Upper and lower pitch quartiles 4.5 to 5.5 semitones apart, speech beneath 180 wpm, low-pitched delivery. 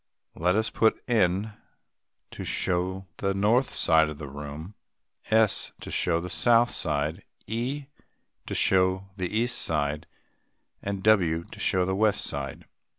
Yes: average, 5.0 semitones; average, 145 wpm; very low, 95 Hz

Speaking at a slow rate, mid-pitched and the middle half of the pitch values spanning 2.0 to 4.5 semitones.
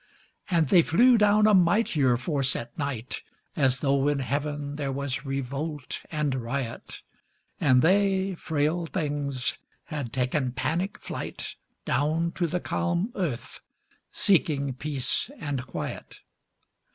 Yes: slow, 125 wpm; medium, 145 Hz; average, 4.2 semitones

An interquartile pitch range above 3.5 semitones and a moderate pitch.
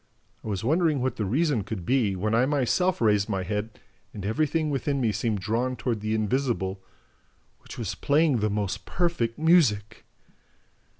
No: wide, 5.4 semitones; low, 115 Hz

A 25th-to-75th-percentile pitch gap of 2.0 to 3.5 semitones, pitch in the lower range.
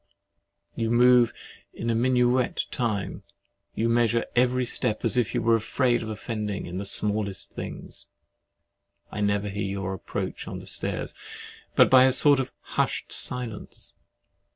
Yes: average, 3.1 semitones; low, 115 Hz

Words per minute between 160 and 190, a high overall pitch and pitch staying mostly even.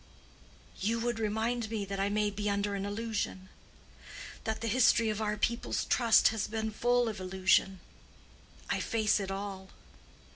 No: average, 150 wpm; high, 210 Hz; narrow, 2.2 semitones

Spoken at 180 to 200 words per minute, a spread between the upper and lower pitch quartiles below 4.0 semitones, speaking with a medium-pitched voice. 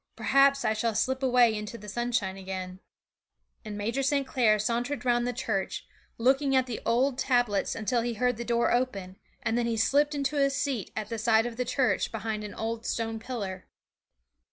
No: average, 190 wpm; average, 3.1 semitones; high, 235 Hz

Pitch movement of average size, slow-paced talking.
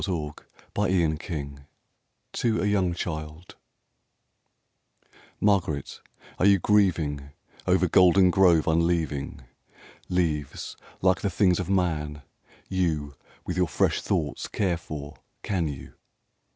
Yes: average, 3.5 semitones; slow, 105 wpm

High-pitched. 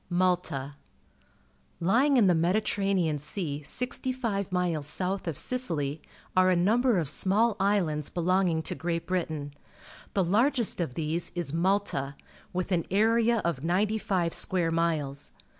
No: medium, 180 Hz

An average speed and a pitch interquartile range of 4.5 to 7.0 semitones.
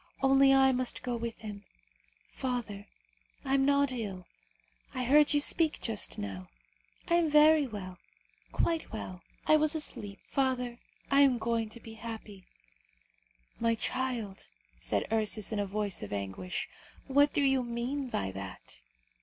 Yes: average, 150 wpm; average, 4.9 semitones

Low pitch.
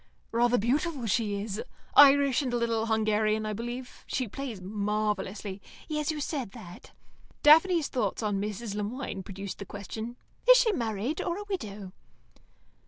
No: high, 225 Hz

